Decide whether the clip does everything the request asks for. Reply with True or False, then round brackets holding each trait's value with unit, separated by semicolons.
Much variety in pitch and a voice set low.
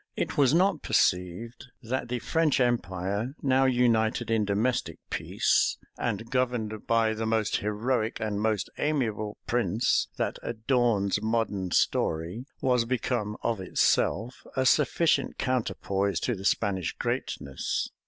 False (3.3 semitones; 115 Hz)